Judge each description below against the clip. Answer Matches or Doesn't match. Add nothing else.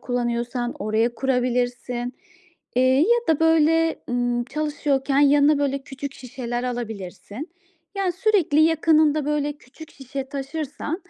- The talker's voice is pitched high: Matches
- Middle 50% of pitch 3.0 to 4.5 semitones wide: Matches